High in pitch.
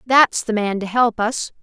Yes: high, 225 Hz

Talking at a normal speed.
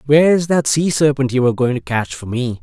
No: fast, 250 wpm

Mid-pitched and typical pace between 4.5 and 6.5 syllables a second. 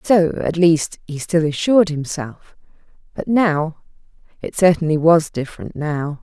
No: medium, 160 Hz; 4.3 syllables/s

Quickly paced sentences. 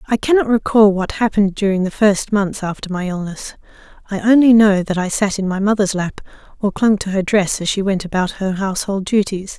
Yes: fast, 215 wpm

